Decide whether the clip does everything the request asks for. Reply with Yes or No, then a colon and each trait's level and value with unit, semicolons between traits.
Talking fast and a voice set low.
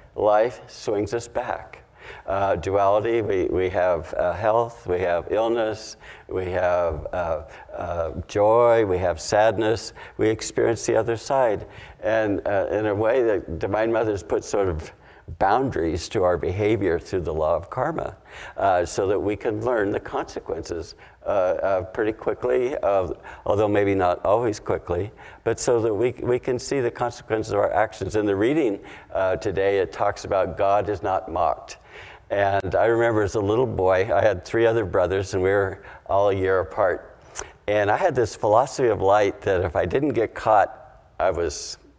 No: average, 175 wpm; low, 105 Hz